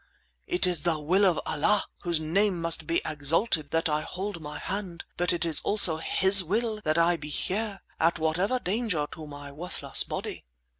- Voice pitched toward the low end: No, medium, 170 Hz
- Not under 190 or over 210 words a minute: No, average, 180 wpm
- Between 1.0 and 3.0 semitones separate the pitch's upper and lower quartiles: No, average, 3.7 semitones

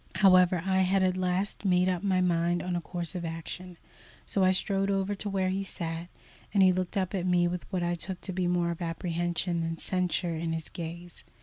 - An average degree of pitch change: No, narrow, 1.6 semitones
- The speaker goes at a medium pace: No, fast, 220 wpm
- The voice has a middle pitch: Yes, medium, 180 Hz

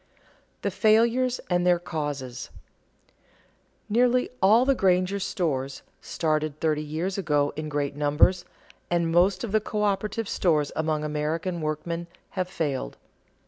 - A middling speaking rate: No, slow, 130 wpm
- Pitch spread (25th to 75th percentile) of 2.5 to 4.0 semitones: No, average, 4.7 semitones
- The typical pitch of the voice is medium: Yes, medium, 170 Hz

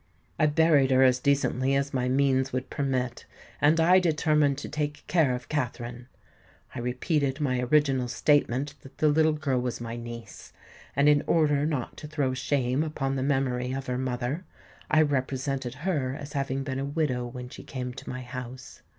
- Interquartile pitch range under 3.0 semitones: Yes, narrow, 2.6 semitones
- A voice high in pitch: No, low, 135 Hz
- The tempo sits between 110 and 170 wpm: No, average, 180 wpm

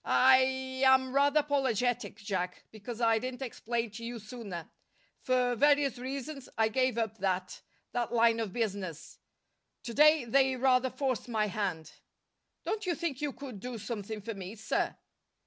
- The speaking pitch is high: Yes, high, 240 Hz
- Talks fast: No, average, 160 wpm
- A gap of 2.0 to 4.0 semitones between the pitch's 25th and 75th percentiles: Yes, average, 3.4 semitones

